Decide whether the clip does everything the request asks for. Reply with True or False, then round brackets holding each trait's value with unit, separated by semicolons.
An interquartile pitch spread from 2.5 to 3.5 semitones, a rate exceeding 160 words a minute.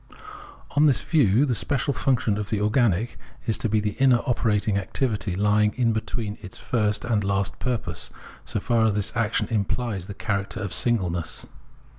True (3.0 semitones; 170 wpm)